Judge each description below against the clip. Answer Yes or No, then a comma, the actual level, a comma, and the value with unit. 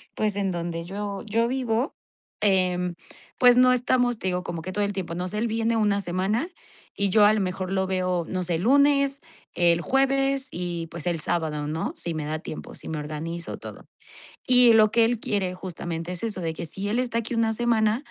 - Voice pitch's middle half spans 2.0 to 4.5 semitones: No, average, 4.9 semitones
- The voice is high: Yes, high, 195 Hz